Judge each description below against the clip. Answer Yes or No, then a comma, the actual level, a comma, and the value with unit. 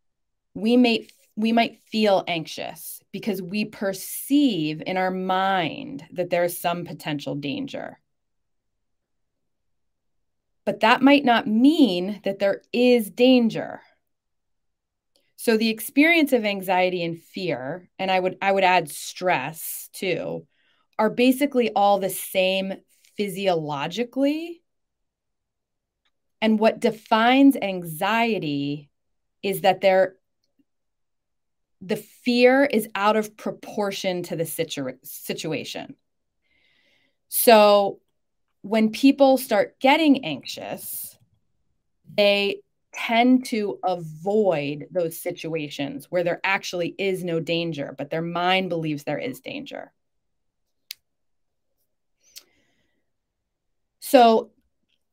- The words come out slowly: Yes, slow, 100 wpm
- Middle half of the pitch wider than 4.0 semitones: Yes, average, 5.1 semitones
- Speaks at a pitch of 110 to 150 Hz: No, high, 195 Hz